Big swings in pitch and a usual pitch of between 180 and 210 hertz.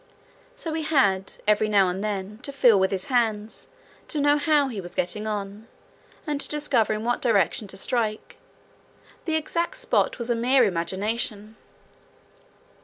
No: wide, 5.8 semitones; high, 220 Hz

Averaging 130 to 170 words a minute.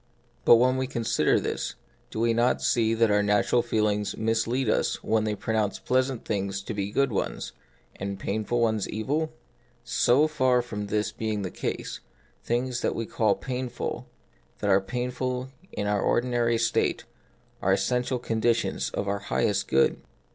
Yes: average, 165 wpm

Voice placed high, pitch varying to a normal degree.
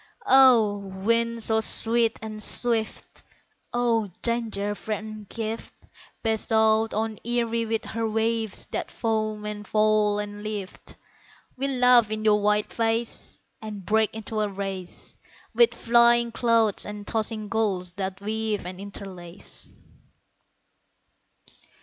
No: high, 220 Hz; narrow, 1.7 semitones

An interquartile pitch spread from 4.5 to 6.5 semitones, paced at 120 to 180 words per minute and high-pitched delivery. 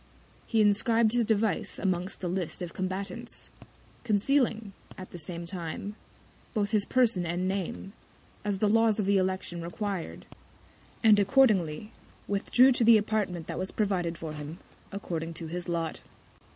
No: average, 3.6 semitones; average, 150 wpm; high, 195 Hz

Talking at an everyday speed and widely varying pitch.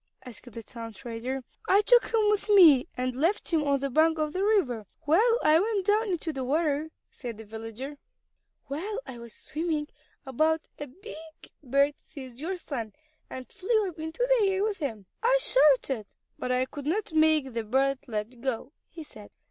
Yes: average, 185 wpm; wide, 6.2 semitones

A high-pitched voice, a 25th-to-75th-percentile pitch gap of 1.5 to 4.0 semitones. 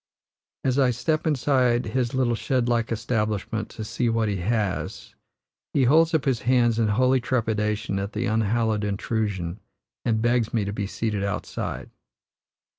No: low, 115 Hz; average, 2.8 semitones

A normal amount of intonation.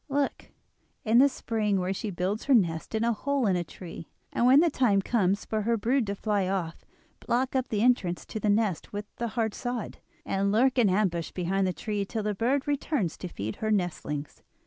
Yes: average, 4.2 semitones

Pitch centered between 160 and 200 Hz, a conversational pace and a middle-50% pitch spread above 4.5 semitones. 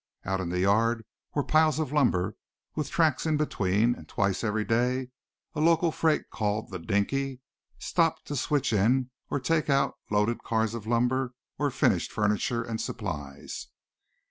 No: low, 120 Hz; average, 160 wpm; wide, 5.5 semitones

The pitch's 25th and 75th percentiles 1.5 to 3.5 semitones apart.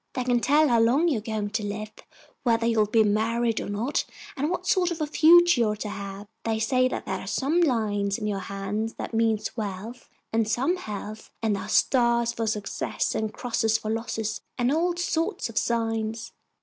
Yes: average, 3.0 semitones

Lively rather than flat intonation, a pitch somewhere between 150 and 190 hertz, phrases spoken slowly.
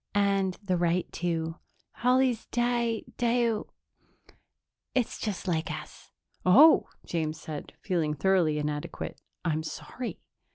Yes: wide, 6.3 semitones; medium, 185 Hz; slow, 110 wpm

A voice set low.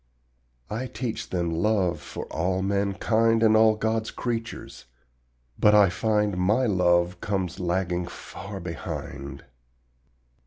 Yes: low, 100 Hz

